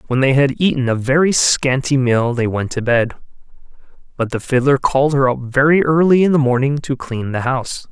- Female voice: No, male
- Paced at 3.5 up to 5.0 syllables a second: No, 5.4 syllables/s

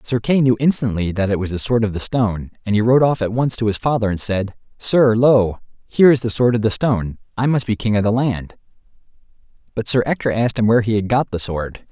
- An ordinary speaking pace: No, fast, 245 wpm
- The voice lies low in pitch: Yes, low, 115 Hz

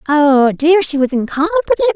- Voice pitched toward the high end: Yes, very high, 315 Hz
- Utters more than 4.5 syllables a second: Yes, 5.1 syllables/s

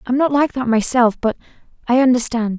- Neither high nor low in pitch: No, high, 245 Hz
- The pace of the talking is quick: No, average, 185 wpm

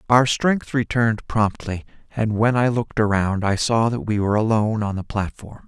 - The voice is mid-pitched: No, low, 110 Hz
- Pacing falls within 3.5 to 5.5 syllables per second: Yes, 5.2 syllables/s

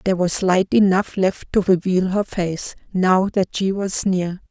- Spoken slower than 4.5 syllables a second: Yes, 4.2 syllables/s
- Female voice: Yes, female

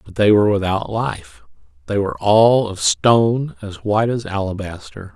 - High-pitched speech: No, low, 105 Hz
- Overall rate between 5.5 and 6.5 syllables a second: No, 4.9 syllables/s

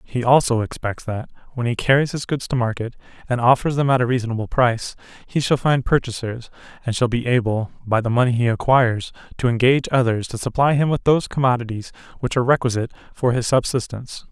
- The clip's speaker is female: No, male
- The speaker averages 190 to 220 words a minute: Yes, average, 195 wpm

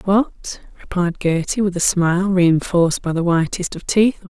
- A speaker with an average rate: Yes, average, 165 wpm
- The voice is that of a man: No, female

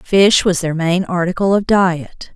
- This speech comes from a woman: Yes, female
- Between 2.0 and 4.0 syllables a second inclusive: Yes, 3.9 syllables/s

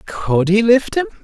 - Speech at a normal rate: Yes, average, 195 wpm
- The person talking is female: No, male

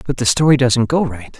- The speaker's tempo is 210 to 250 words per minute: No, fast, 260 wpm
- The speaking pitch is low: Yes, low, 130 Hz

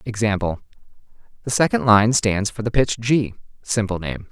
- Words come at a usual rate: Yes, average, 155 wpm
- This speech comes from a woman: No, male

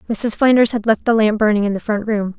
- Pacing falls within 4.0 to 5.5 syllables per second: No, 5.9 syllables/s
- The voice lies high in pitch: Yes, high, 215 Hz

